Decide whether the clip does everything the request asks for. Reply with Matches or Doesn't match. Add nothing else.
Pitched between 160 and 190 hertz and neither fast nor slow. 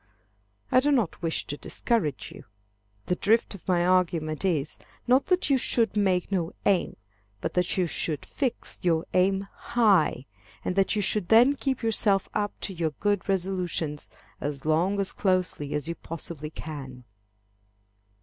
Matches